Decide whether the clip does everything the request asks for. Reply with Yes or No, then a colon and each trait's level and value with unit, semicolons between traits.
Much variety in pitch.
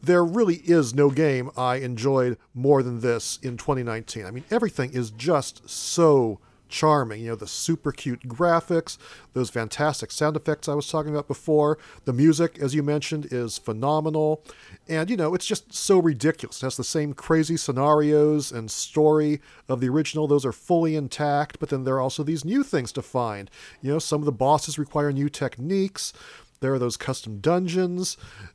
No: average, 3.7 semitones